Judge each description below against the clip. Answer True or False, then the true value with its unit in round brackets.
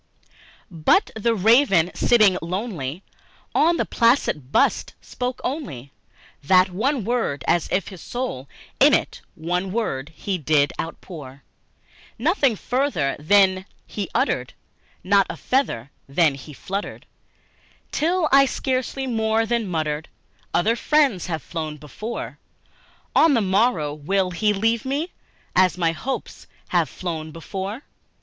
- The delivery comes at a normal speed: False (130 wpm)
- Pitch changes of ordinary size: False (7.0 semitones)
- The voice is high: True (195 Hz)